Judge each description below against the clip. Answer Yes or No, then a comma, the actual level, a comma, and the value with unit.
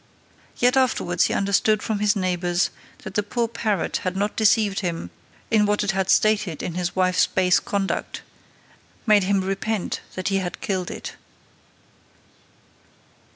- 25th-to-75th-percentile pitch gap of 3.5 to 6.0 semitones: No, narrow, 2.5 semitones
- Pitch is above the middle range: Yes, high, 195 Hz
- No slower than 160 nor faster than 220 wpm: No, average, 150 wpm